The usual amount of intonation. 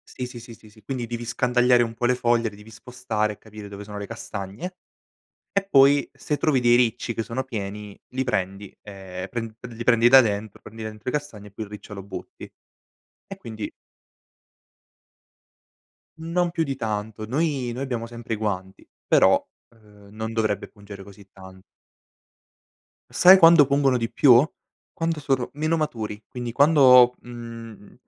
Yes: average, 3.7 semitones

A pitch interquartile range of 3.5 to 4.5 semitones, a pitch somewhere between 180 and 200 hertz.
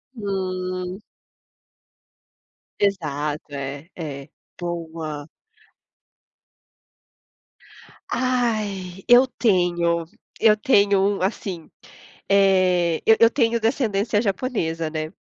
Yes: average, 4.2 semitones; medium, 185 Hz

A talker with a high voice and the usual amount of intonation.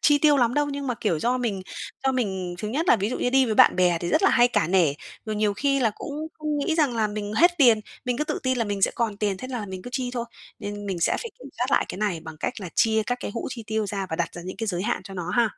Yes: high, 220 Hz; average, 4.8 semitones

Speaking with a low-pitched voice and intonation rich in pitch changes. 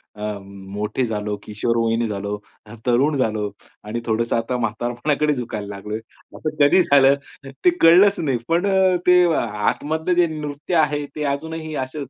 Yes: low, 130 Hz; wide, 6.3 semitones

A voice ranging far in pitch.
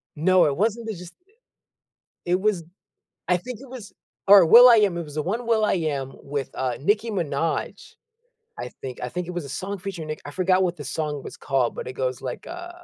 Yes: wide, 6.4 semitones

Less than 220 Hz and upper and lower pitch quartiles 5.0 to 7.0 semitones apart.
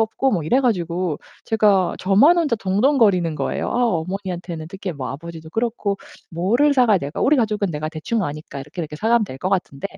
Yes: high, 190 Hz; wide, 5.5 semitones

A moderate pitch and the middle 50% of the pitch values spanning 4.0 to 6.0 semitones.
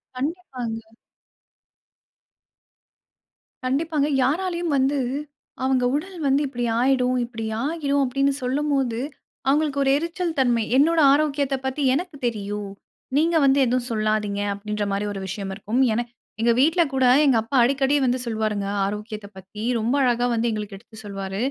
No: very high, 255 Hz; average, 4.7 semitones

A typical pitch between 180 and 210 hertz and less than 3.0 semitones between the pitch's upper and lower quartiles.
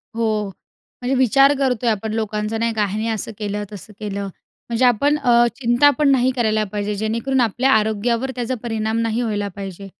No: high, 225 Hz; narrow, 2.6 semitones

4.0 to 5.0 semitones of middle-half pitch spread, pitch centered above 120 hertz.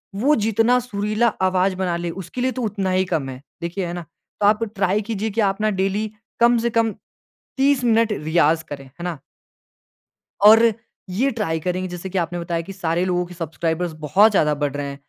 Yes: average, 4.3 semitones; medium, 185 Hz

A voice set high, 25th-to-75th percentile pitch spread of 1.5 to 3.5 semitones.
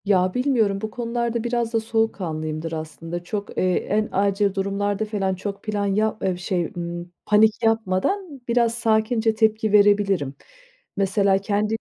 Yes: high, 205 Hz; average, 2.9 semitones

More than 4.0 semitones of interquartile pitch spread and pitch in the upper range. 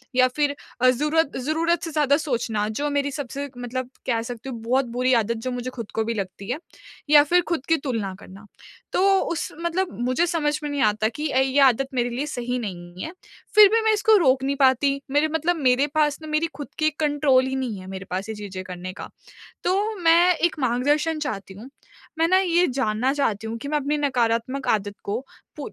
Yes: average, 4.7 semitones; very high, 265 Hz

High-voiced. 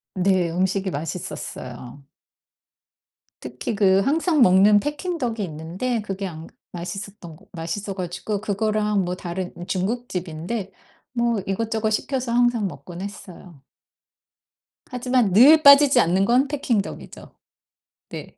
Yes: high, 200 Hz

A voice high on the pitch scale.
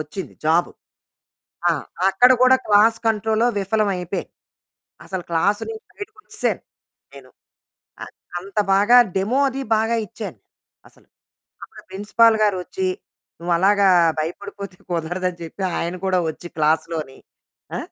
Yes: high, 200 Hz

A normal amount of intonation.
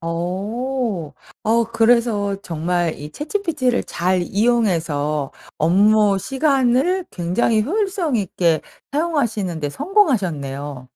No: wide, 7.5 semitones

